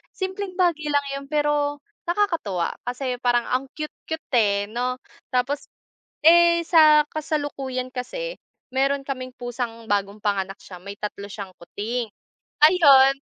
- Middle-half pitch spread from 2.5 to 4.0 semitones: No, average, 4.7 semitones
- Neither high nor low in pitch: No, very high, 265 Hz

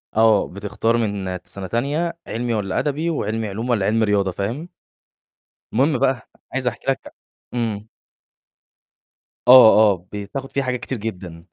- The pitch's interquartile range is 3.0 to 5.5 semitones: Yes, average, 4.3 semitones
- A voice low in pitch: Yes, low, 115 Hz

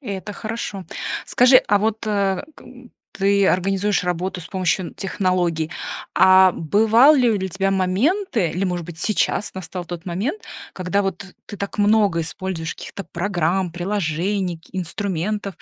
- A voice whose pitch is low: No, high, 190 Hz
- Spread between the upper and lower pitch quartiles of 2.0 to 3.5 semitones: Yes, narrow, 2.5 semitones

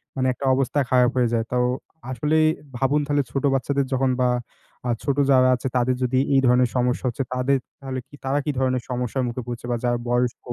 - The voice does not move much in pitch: Yes, narrow, 1.6 semitones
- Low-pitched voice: Yes, low, 130 Hz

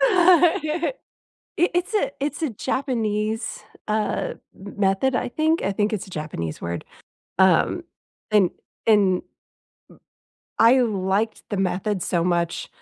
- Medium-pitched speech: No, high, 215 Hz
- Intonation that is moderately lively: No, wide, 7.7 semitones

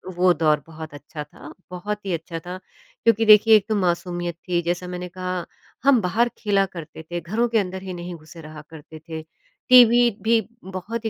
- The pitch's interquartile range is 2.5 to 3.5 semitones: No, average, 3.9 semitones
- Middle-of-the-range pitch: Yes, medium, 180 Hz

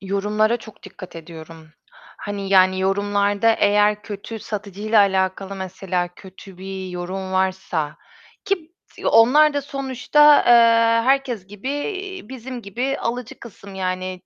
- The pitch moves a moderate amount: Yes, average, 4.0 semitones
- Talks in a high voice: Yes, high, 205 Hz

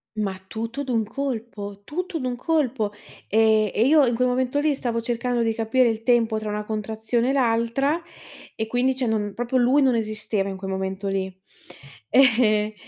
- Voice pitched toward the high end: Yes, high, 230 Hz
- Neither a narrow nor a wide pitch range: Yes, average, 3.0 semitones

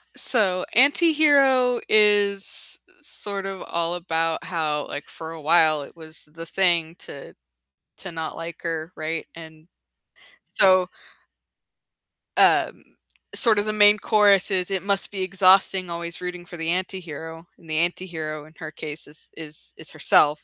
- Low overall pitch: No, medium, 175 Hz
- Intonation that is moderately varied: Yes, average, 3.5 semitones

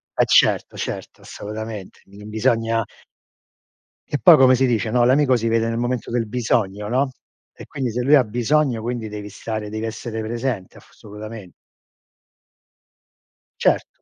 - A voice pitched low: Yes, low, 115 Hz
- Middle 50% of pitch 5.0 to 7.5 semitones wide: No, narrow, 2.5 semitones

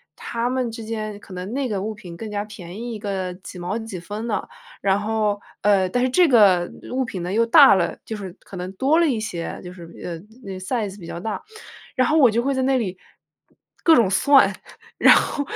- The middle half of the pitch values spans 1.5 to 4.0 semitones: No, average, 4.4 semitones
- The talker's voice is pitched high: Yes, high, 210 Hz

